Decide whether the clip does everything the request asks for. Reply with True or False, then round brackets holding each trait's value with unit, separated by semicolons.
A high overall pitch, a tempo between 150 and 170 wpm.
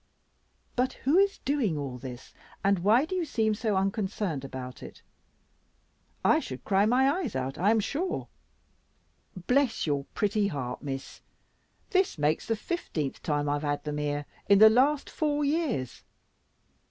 True (205 Hz; 155 wpm)